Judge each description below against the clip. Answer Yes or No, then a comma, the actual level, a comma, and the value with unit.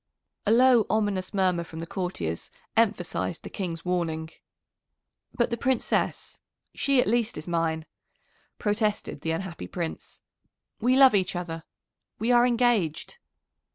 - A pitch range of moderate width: No, wide, 5.8 semitones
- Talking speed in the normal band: No, slow, 130 wpm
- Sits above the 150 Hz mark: Yes, high, 190 Hz